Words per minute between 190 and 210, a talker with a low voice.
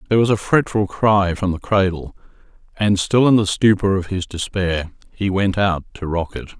Yes: average, 200 wpm; very low, 95 Hz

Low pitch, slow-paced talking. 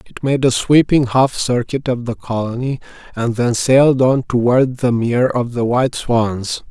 No: low, 125 Hz; average, 180 wpm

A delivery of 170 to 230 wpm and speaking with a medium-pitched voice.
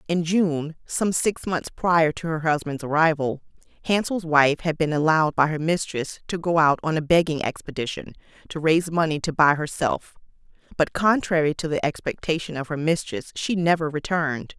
Yes: average, 175 wpm; medium, 160 Hz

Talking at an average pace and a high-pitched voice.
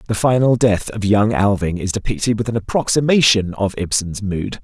No: average, 180 wpm; low, 105 Hz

